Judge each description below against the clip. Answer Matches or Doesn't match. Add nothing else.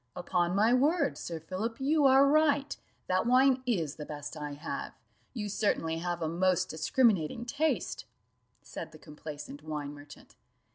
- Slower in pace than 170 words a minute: Matches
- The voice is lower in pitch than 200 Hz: Matches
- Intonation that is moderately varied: Doesn't match